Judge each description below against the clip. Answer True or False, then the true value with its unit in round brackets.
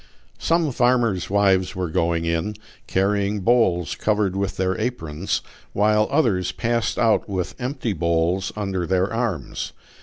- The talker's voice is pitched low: True (100 Hz)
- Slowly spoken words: True (130 wpm)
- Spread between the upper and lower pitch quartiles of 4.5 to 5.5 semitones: False (3.9 semitones)